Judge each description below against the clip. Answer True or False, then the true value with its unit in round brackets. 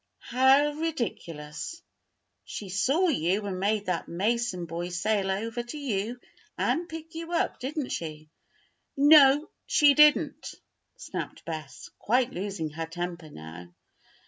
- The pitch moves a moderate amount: False (8.8 semitones)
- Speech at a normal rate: False (125 wpm)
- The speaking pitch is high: True (215 Hz)